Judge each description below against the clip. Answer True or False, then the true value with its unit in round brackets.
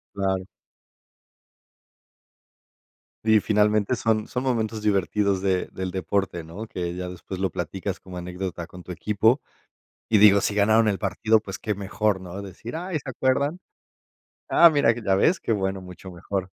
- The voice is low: True (100 Hz)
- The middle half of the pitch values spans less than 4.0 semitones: True (2.9 semitones)